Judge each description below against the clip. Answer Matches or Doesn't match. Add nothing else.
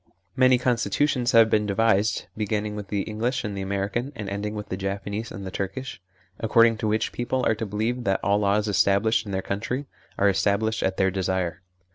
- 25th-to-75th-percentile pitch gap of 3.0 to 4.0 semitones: Doesn't match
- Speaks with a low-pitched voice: Matches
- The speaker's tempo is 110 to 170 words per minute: Doesn't match